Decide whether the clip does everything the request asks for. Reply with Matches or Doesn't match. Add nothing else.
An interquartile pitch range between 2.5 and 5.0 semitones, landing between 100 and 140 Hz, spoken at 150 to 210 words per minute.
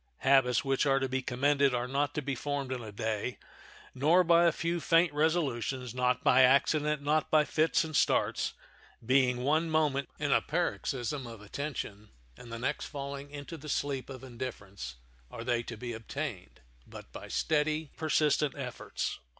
Matches